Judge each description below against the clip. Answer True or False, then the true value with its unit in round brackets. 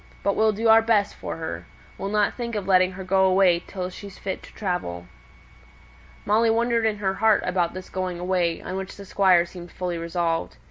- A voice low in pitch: False (190 Hz)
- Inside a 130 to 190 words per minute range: False (200 wpm)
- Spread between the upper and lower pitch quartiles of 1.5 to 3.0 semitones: True (2.7 semitones)